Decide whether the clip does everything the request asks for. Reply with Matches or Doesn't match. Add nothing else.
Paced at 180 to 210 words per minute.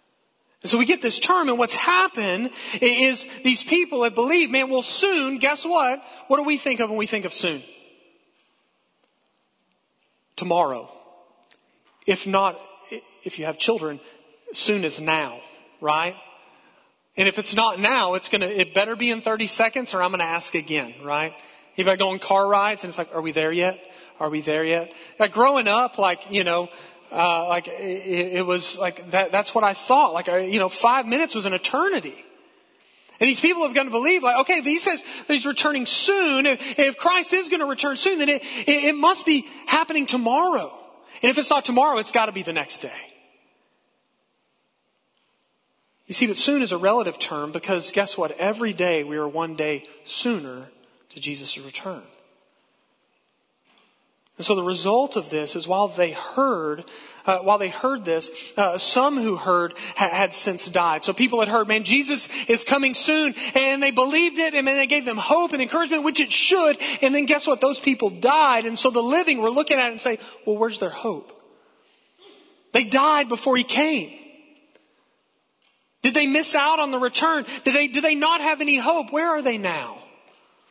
Matches